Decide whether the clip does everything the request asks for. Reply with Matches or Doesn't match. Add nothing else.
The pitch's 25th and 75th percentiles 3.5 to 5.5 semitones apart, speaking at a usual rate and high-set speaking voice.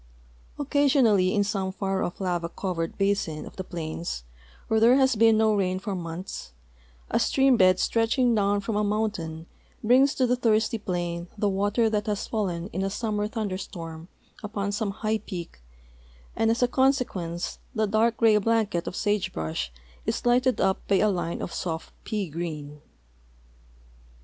Matches